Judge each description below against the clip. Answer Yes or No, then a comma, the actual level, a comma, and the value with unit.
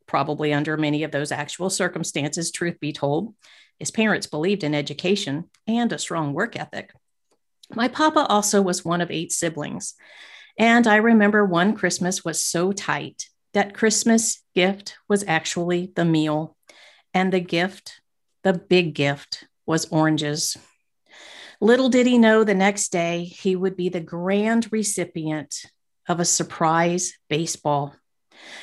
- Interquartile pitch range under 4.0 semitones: No, average, 4.4 semitones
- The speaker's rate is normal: Yes, average, 145 wpm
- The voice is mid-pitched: Yes, medium, 180 Hz